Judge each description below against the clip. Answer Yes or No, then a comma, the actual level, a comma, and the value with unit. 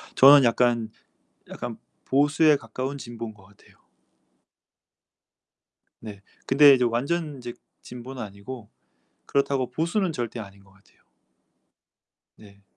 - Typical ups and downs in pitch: Yes, average, 4.2 semitones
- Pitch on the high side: No, low, 125 Hz